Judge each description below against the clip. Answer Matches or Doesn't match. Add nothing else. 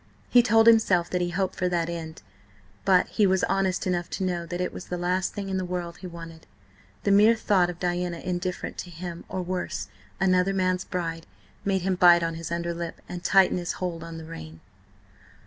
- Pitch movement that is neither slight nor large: Doesn't match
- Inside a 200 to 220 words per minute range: Matches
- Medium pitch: Matches